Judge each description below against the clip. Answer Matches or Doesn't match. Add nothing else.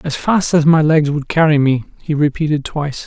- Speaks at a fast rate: Matches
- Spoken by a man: Matches